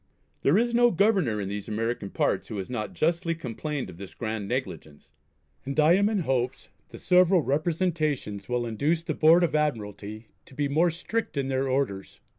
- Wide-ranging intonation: Yes, wide, 7.3 semitones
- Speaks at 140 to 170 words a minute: No, average, 185 wpm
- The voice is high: No, medium, 140 Hz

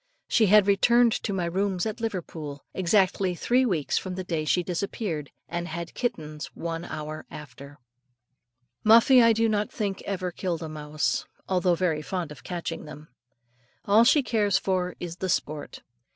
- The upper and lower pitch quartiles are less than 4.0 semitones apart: No, average, 4.5 semitones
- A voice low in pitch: No, medium, 180 Hz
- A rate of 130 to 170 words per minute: Yes, average, 165 wpm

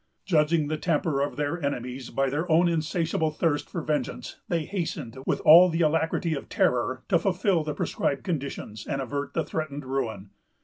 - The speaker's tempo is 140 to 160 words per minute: No, average, 175 wpm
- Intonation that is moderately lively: Yes, average, 3.2 semitones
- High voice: No, medium, 155 Hz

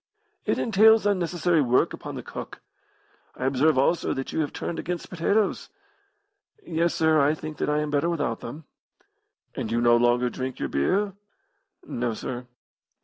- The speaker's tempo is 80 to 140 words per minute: No, average, 160 wpm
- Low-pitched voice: No, medium, 150 Hz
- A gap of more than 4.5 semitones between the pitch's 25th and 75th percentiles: Yes, wide, 5.5 semitones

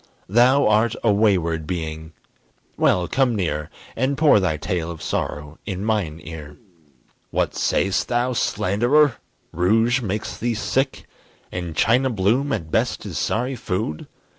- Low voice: Yes, low, 105 Hz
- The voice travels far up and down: Yes, wide, 6.3 semitones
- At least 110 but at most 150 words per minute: Yes, average, 140 wpm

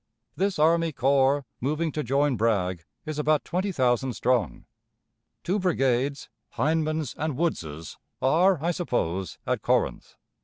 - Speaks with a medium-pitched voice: Yes, medium, 145 Hz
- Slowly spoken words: Yes, slow, 125 wpm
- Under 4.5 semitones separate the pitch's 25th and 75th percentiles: No, average, 4.8 semitones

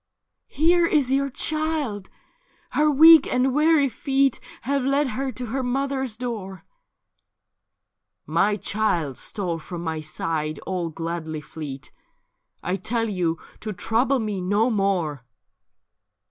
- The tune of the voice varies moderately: No, wide, 7.9 semitones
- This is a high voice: Yes, high, 220 Hz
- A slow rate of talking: Yes, slow, 130 wpm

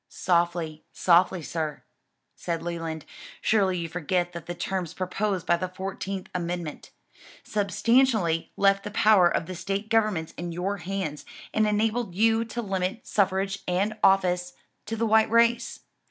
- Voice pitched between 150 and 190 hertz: Yes, medium, 185 Hz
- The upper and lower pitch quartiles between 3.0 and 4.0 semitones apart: Yes, average, 3.4 semitones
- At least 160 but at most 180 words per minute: No, average, 145 wpm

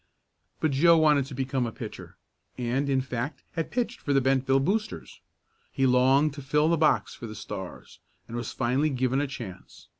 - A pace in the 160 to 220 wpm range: Yes, average, 185 wpm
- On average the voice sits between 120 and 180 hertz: Yes, low, 135 Hz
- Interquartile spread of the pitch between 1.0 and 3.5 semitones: Yes, average, 2.8 semitones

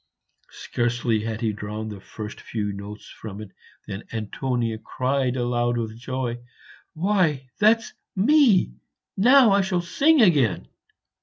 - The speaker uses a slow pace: Yes, slow, 130 wpm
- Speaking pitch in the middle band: No, low, 120 Hz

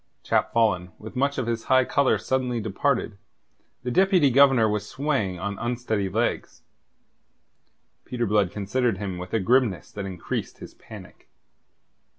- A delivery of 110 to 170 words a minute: Yes, average, 145 wpm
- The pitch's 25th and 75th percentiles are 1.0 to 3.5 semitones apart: No, average, 4.6 semitones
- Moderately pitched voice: No, low, 115 Hz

